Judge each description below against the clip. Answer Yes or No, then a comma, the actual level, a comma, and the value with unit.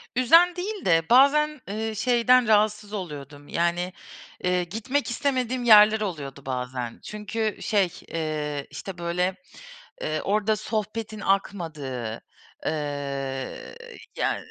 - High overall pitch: Yes, high, 200 Hz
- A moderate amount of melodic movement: No, wide, 7.0 semitones